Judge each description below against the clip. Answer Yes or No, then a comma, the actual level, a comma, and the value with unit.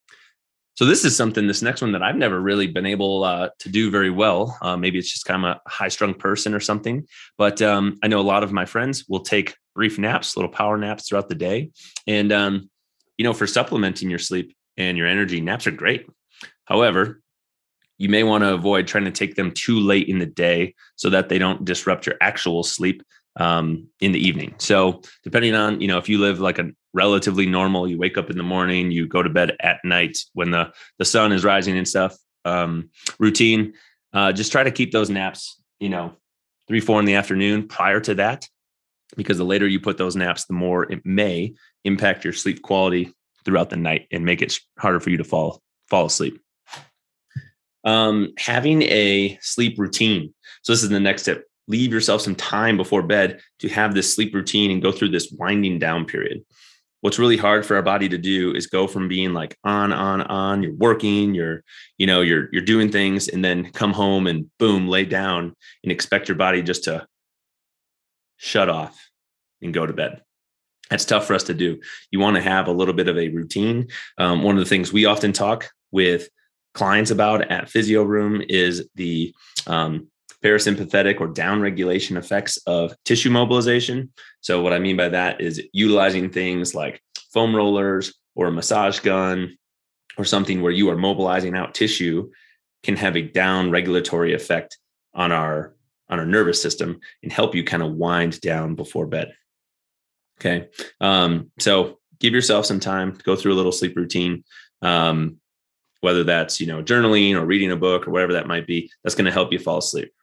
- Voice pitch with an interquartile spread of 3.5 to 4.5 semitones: No, average, 2.7 semitones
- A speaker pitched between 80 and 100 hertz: Yes, very low, 95 Hz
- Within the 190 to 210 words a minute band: Yes, average, 200 wpm